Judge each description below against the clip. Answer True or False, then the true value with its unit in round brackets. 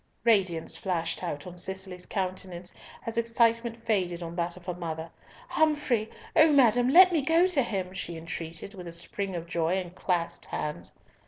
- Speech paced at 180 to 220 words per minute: False (170 wpm)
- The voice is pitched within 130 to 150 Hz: False (185 Hz)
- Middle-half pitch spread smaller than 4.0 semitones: False (5.2 semitones)